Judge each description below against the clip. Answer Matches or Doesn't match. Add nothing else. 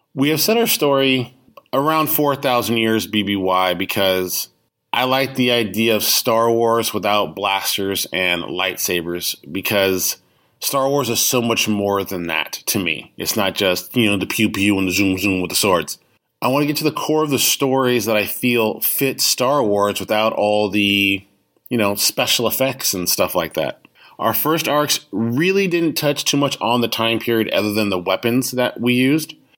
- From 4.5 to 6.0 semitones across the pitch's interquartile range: Matches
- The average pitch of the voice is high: Doesn't match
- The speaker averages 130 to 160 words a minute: Doesn't match